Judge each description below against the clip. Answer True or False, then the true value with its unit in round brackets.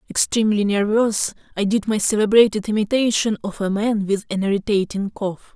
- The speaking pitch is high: True (210 Hz)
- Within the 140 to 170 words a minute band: True (150 wpm)